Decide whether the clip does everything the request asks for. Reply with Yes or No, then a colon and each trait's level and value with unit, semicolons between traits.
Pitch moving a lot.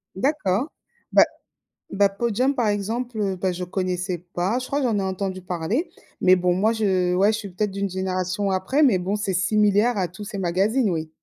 No: average, 2.9 semitones